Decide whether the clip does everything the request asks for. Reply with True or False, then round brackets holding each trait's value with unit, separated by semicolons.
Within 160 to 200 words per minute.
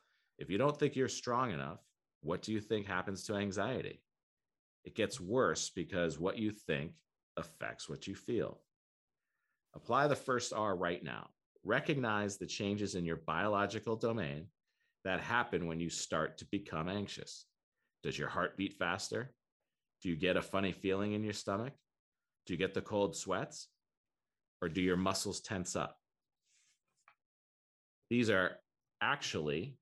False (150 wpm)